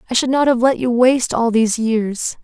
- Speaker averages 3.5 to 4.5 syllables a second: No, 5.5 syllables/s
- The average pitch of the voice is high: Yes, high, 240 Hz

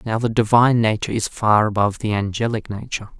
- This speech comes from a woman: No, male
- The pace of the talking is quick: No, average, 190 wpm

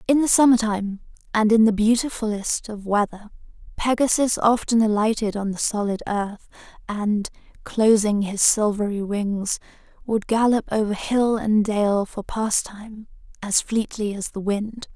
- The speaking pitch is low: No, high, 215 Hz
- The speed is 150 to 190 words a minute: No, average, 140 wpm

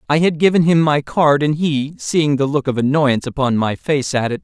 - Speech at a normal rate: No, fast, 230 wpm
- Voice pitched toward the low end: No, medium, 145 Hz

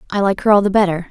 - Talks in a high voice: Yes, high, 195 Hz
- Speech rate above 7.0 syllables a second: Yes, 8.1 syllables/s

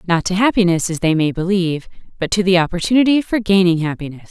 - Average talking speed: Yes, average, 195 wpm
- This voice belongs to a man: No, female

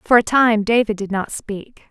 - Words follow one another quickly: Yes, fast, 220 wpm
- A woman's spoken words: Yes, female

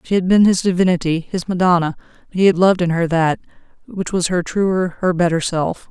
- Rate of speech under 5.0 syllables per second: No, 5.4 syllables/s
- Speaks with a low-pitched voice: No, medium, 180 Hz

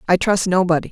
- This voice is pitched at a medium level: Yes, medium, 180 Hz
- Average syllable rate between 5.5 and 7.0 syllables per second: Yes, 6.7 syllables/s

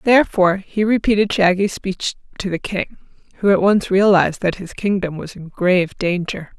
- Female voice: Yes, female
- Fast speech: No, average, 175 wpm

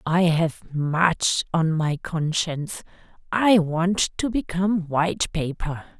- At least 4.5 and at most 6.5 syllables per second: No, 3.6 syllables/s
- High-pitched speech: No, medium, 170 Hz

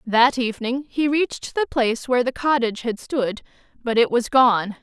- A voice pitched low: No, very high, 250 Hz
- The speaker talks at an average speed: Yes, average, 185 wpm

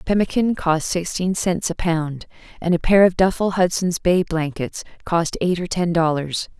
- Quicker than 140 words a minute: Yes, average, 175 wpm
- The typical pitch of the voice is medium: Yes, medium, 175 Hz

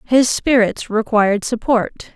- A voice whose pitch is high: Yes, high, 230 Hz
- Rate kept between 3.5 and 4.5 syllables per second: Yes, 4.0 syllables/s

